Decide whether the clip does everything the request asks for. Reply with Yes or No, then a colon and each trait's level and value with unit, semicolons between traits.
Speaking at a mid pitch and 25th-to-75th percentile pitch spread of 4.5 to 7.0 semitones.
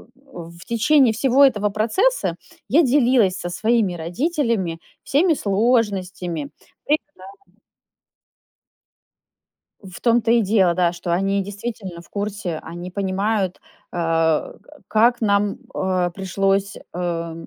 No: high, 200 Hz; average, 4.9 semitones